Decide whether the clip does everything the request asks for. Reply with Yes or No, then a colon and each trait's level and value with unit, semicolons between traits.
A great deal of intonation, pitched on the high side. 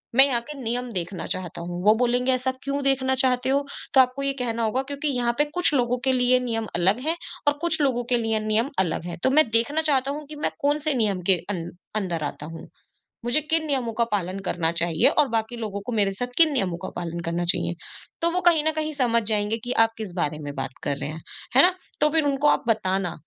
Yes: wide, 6.5 semitones; high, 240 Hz